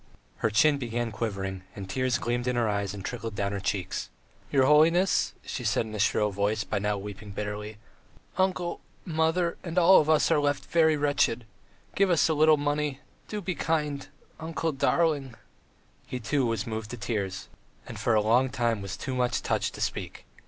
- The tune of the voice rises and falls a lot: Yes, wide, 6.6 semitones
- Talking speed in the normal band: Yes, average, 190 wpm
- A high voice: No, low, 125 Hz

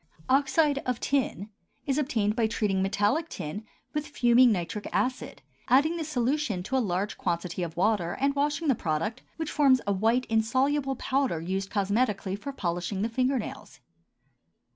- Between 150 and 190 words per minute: Yes, average, 160 wpm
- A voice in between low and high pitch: No, high, 230 Hz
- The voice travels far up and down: Yes, wide, 5.7 semitones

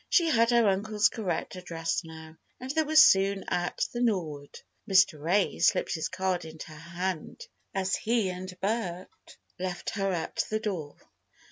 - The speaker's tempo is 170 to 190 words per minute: No, average, 160 wpm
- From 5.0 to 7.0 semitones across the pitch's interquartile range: No, average, 4.0 semitones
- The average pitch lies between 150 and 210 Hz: Yes, high, 190 Hz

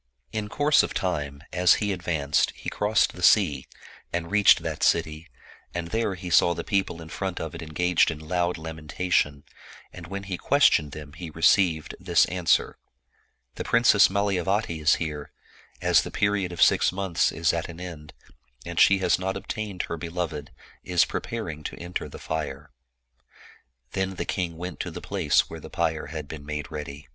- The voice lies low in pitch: Yes, very low, 85 Hz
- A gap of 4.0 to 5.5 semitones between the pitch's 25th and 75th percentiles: No, average, 3.6 semitones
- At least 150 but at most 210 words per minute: Yes, average, 180 wpm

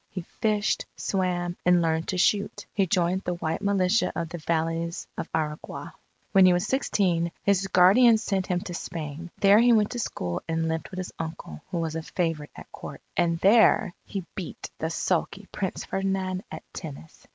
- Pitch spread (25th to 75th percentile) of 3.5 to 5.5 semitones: No, average, 2.9 semitones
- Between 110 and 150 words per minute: No, average, 185 wpm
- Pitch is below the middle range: No, medium, 180 Hz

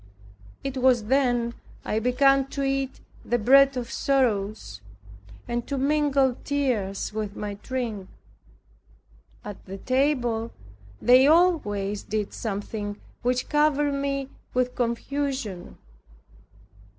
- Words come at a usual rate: No, slow, 105 wpm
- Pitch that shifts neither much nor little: Yes, average, 4.3 semitones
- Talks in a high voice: Yes, very high, 250 Hz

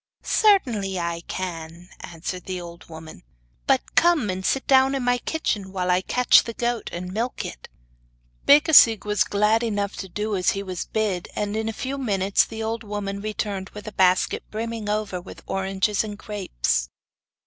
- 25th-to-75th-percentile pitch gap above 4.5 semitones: No, average, 3.4 semitones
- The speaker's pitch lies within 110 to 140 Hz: No, high, 205 Hz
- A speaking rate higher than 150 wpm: Yes, average, 175 wpm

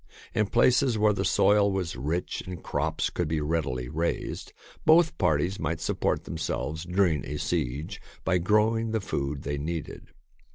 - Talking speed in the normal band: Yes, average, 160 wpm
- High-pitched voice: No, very low, 85 Hz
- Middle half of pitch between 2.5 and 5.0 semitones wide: No, wide, 5.4 semitones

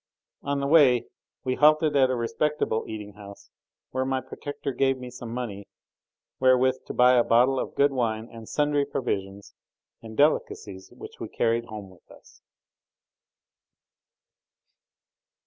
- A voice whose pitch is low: Yes, low, 125 Hz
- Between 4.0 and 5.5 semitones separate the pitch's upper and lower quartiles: No, average, 3.6 semitones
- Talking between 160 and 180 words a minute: No, average, 140 wpm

